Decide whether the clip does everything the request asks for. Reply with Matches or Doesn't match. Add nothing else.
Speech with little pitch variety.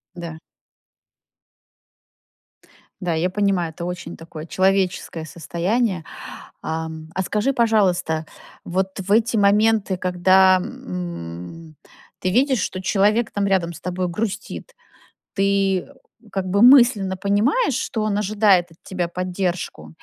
Doesn't match